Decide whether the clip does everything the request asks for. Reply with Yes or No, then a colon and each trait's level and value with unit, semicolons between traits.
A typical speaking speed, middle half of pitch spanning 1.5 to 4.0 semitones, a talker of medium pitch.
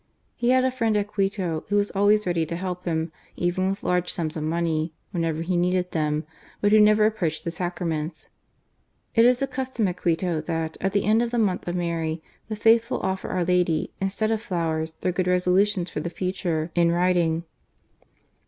Yes: average, 195 wpm; average, 3.7 semitones; medium, 180 Hz